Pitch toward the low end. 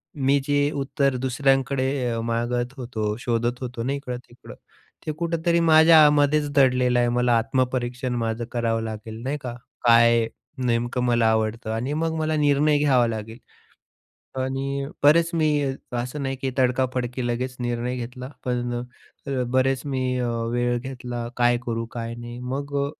Yes: low, 125 Hz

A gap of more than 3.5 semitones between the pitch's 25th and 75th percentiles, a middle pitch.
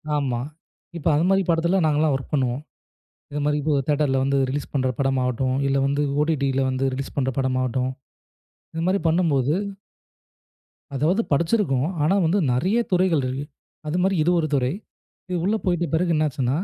Yes: average, 4.0 semitones; medium, 145 Hz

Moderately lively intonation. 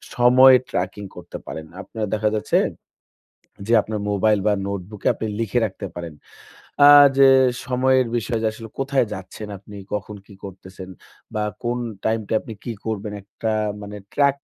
Yes: average, 3.1 semitones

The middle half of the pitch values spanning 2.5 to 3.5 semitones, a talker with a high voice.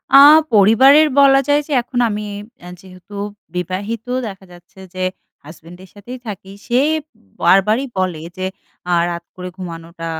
No: average, 4.4 semitones; high, 195 Hz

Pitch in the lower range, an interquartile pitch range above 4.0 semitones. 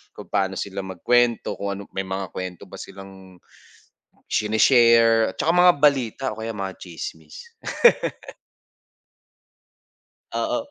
No: low, 100 Hz; average, 3.6 semitones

